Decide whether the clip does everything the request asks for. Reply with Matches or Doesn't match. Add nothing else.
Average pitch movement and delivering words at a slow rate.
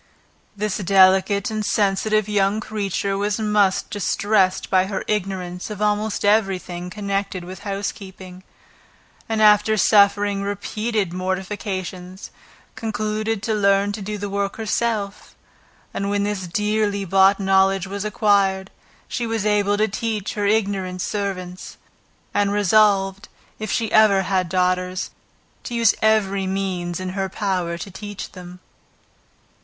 Doesn't match